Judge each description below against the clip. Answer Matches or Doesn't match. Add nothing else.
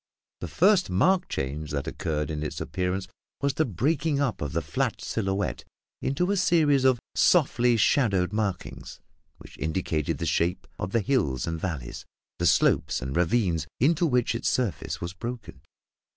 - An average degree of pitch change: Doesn't match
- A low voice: Matches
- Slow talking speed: Doesn't match